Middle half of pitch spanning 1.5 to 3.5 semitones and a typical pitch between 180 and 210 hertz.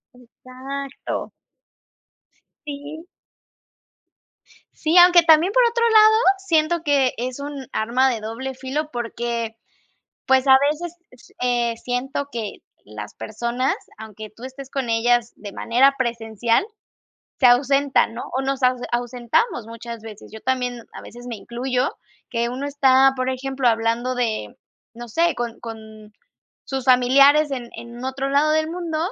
No: average, 3.0 semitones; very high, 255 Hz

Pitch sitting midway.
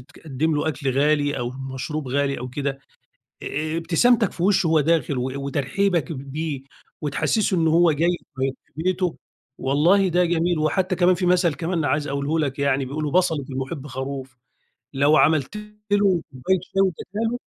Yes: medium, 155 Hz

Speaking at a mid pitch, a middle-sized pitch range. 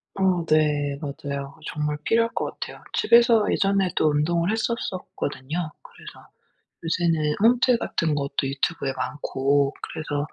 Yes: medium, 155 Hz; average, 4.9 semitones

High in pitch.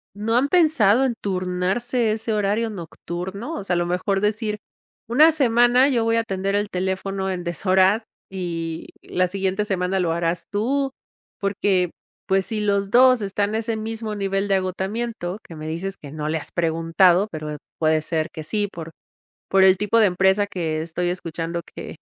Yes: high, 195 Hz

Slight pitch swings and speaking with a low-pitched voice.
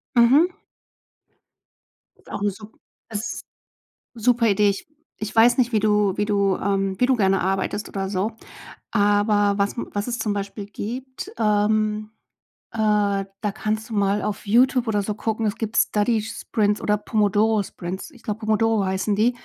No: narrow, 1.8 semitones; high, 210 Hz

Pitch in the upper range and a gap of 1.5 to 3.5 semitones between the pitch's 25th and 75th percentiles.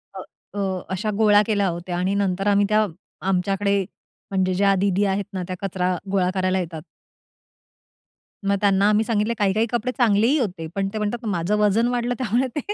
Yes: high, 200 Hz; narrow, 2.4 semitones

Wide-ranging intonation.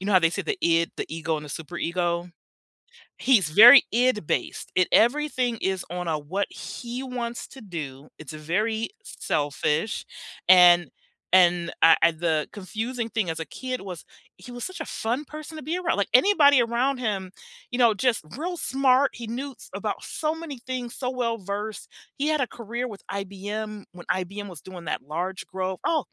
Yes: wide, 6.3 semitones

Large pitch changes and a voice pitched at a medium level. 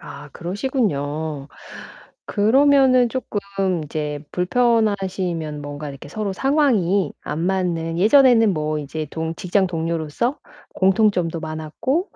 Yes: wide, 6.3 semitones; medium, 180 Hz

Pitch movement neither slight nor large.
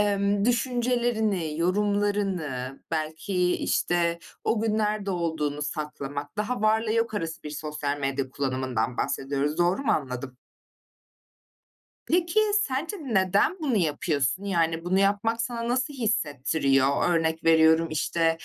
No: wide, 6.4 semitones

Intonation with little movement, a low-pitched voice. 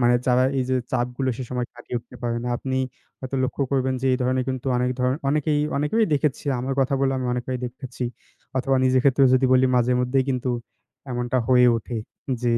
Yes: narrow, 1.3 semitones; low, 130 Hz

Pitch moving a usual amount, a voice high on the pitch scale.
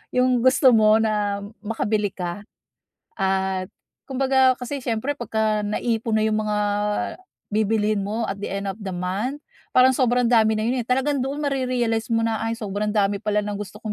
Yes: average, 3.3 semitones; high, 220 Hz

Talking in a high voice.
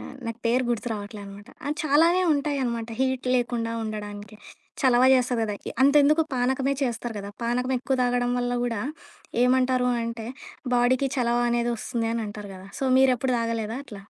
Yes: high, 245 Hz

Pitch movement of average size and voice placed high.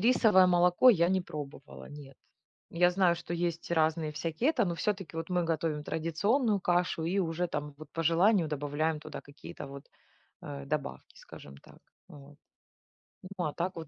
No: average, 3.0 semitones; medium, 165 Hz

